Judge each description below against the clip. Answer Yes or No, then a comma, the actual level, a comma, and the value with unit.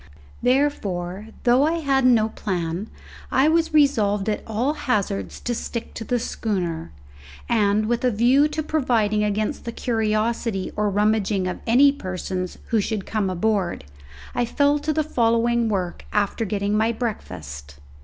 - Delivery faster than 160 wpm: No, average, 150 wpm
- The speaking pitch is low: No, high, 220 Hz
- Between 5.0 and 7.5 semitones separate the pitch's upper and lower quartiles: No, average, 3.8 semitones